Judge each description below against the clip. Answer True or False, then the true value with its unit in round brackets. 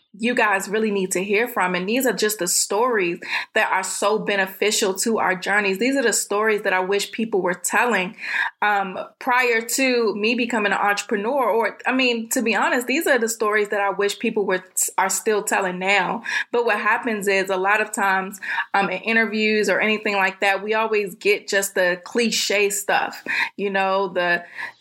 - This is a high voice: True (210 Hz)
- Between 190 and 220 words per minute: True (200 wpm)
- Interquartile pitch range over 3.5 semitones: False (2.8 semitones)